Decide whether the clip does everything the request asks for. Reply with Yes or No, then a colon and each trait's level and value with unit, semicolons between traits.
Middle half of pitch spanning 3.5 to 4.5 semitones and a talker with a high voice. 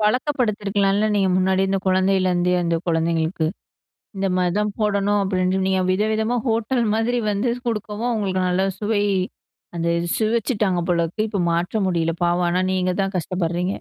No: average, 2.9 semitones; high, 195 Hz